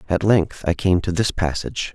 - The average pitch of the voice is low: Yes, very low, 90 Hz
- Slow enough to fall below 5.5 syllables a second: Yes, 5.2 syllables/s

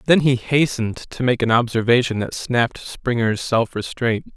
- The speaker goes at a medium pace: Yes, average, 165 wpm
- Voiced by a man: Yes, male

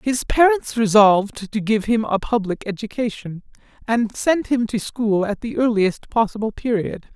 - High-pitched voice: Yes, high, 220 Hz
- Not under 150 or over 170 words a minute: Yes, average, 160 wpm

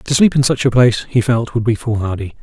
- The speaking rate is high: Yes, fast, 270 wpm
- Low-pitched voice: Yes, low, 120 Hz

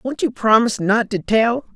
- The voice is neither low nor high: No, high, 230 Hz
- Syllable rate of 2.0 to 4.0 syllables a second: No, 4.9 syllables/s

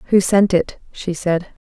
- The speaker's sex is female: Yes, female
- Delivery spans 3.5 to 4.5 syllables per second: Yes, 4.2 syllables/s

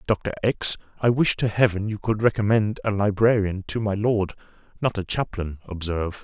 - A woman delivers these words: No, male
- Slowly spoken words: No, average, 165 wpm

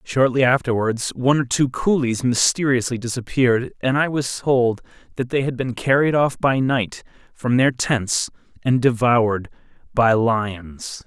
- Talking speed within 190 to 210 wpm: No, average, 145 wpm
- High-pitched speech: No, low, 125 Hz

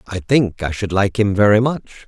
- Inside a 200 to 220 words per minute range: No, fast, 230 wpm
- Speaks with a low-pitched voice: Yes, low, 105 Hz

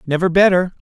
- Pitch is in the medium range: Yes, medium, 180 Hz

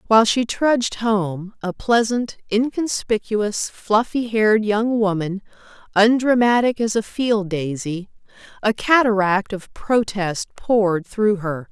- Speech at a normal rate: No, slow, 110 wpm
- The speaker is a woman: Yes, female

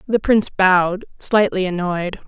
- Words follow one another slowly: Yes, slow, 130 wpm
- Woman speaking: Yes, female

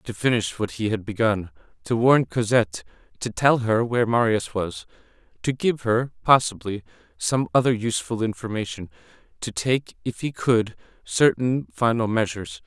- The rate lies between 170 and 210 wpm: No, average, 145 wpm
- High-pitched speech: No, low, 115 Hz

